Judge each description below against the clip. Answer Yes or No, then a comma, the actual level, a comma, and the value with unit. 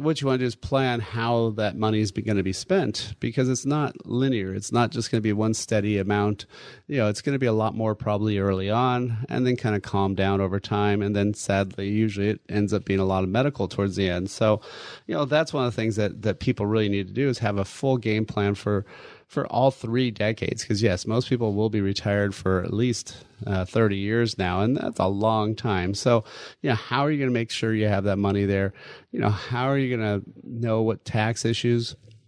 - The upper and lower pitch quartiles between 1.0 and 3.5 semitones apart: Yes, average, 3.1 semitones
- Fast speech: Yes, fast, 250 wpm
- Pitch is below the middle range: Yes, low, 110 Hz